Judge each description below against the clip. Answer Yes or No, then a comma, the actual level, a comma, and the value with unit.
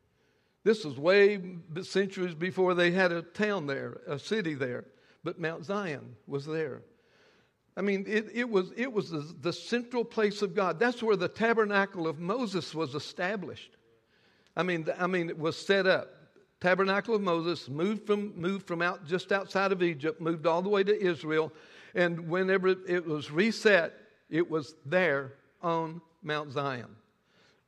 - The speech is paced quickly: No, average, 165 wpm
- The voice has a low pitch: No, medium, 180 Hz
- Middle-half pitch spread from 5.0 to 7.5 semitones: No, average, 3.6 semitones